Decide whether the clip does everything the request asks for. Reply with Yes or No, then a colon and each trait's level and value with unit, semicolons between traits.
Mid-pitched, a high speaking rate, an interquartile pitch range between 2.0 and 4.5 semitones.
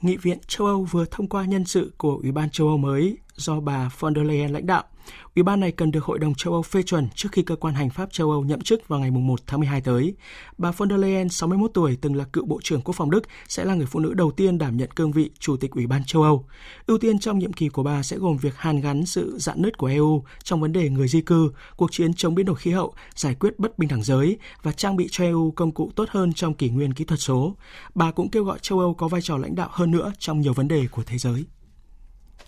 Yes: medium, 160 Hz; fast, 280 wpm; average, 4.1 semitones